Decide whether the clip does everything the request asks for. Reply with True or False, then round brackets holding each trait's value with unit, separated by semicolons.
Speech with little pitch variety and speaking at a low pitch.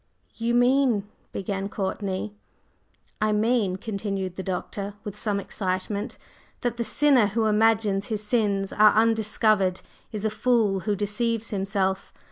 False (2.3 semitones; 210 Hz)